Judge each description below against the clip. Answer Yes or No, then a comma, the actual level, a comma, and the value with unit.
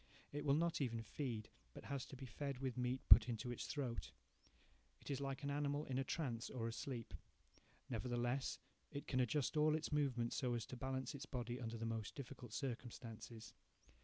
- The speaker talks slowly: No, average, 190 wpm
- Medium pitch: No, low, 130 Hz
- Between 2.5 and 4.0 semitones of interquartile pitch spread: Yes, average, 3.1 semitones